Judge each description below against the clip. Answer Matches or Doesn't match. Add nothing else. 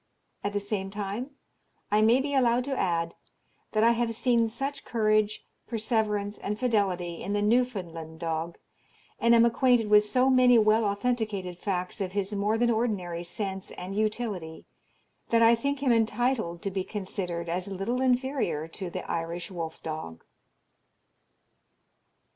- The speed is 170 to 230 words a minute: Doesn't match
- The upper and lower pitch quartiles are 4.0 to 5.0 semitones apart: Matches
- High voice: Matches